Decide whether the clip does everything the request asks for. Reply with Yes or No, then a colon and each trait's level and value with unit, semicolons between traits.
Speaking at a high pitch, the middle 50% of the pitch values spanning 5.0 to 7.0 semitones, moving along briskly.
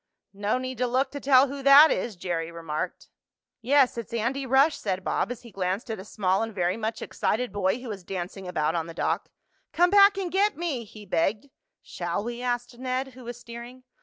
Yes: high, 235 Hz; average, 5.3 semitones; fast, 210 wpm